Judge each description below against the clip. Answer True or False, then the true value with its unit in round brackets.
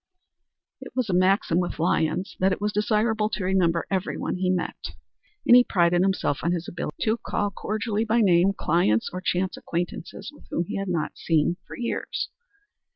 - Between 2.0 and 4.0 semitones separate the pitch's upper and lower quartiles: True (3.3 semitones)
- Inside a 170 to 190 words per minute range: True (175 wpm)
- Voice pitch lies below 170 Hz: False (185 Hz)